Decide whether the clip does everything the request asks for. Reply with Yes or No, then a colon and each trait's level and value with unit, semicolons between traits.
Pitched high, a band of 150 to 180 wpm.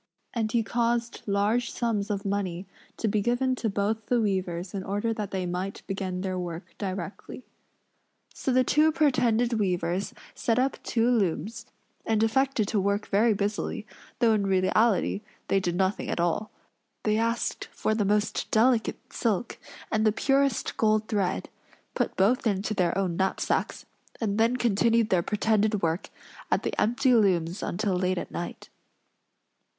Yes: high, 210 Hz; average, 155 wpm